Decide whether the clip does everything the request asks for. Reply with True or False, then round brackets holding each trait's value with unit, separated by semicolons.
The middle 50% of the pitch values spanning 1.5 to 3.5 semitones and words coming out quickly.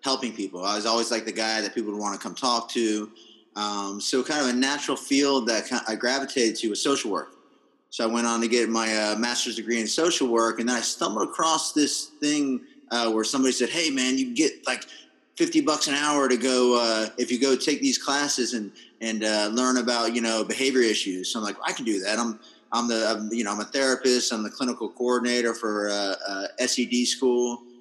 True (3.1 semitones; 235 wpm)